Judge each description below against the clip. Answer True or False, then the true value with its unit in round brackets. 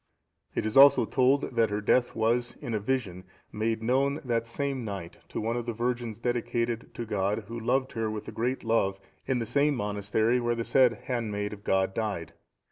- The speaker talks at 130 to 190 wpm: False (200 wpm)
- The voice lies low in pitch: True (115 Hz)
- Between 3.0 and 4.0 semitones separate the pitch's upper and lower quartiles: False (2.6 semitones)